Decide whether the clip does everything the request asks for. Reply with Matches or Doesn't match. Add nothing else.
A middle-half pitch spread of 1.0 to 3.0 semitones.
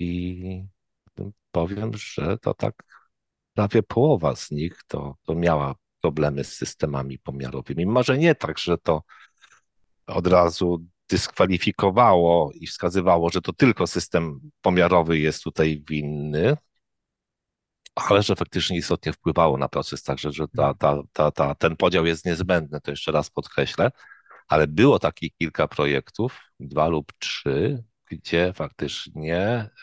Doesn't match